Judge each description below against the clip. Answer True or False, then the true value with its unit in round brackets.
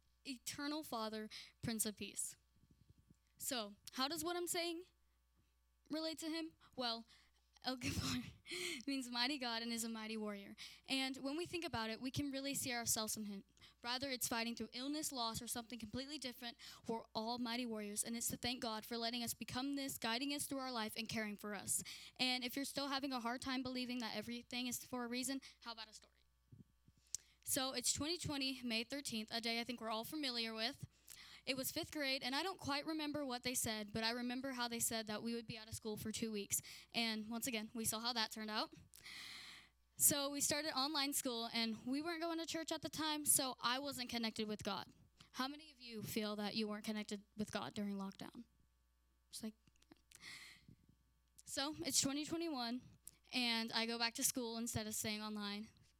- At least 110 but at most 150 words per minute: False (200 wpm)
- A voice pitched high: True (240 Hz)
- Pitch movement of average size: True (3.7 semitones)